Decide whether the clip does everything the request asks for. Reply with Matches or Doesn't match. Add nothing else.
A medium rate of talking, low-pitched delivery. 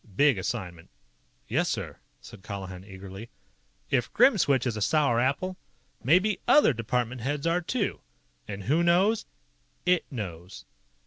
Doesn't match